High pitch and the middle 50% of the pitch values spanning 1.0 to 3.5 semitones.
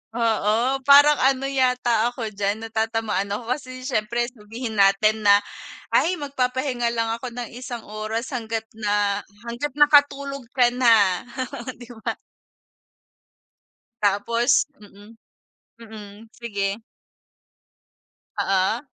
Yes: high, 230 Hz; average, 3.1 semitones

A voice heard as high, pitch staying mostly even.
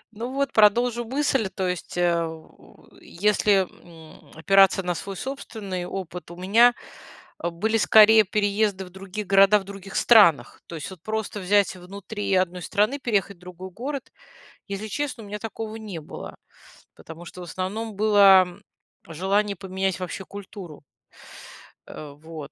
No: high, 195 Hz; average, 3.1 semitones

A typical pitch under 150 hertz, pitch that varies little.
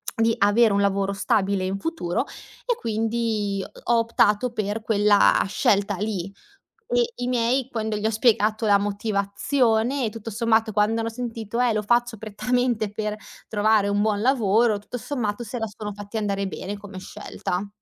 No: high, 215 Hz; narrow, 2.3 semitones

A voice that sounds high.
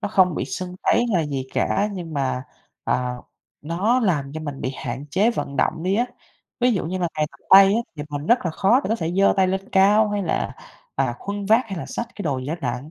No: medium, 180 Hz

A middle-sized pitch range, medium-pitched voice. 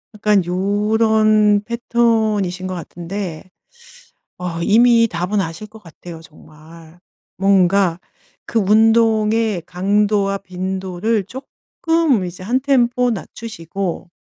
No: average, 3.7 semitones; high, 200 Hz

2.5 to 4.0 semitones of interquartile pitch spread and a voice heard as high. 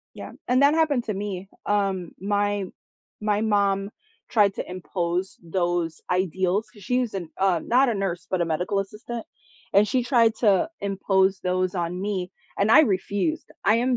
Yes: average, 2.9 semitones; high, 195 Hz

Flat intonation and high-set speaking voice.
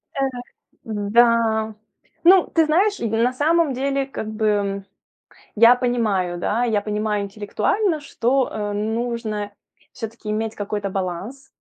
No: average, 3.5 semitones; high, 225 Hz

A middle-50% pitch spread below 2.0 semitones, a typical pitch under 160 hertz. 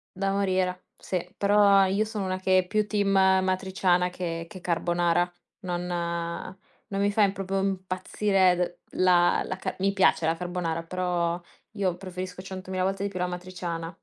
No: narrow, 1.6 semitones; medium, 185 Hz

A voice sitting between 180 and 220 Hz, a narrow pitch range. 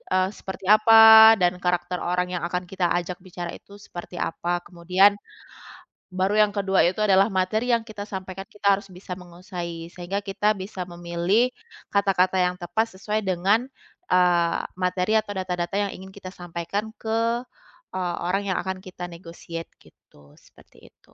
Yes: medium, 185 Hz; narrow, 2.2 semitones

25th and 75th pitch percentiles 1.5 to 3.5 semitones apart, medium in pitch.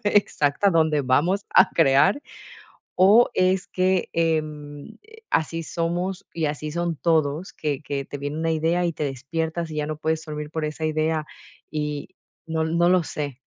Yes: narrow, 2.4 semitones; medium, 160 Hz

